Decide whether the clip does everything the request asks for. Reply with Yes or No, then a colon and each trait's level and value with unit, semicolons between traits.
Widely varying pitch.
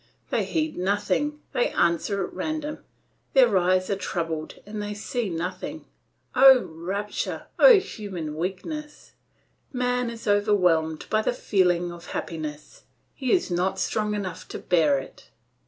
Yes: wide, 6.0 semitones